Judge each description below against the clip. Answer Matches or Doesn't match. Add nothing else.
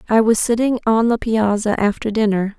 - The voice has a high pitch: Matches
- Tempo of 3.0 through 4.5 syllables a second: Doesn't match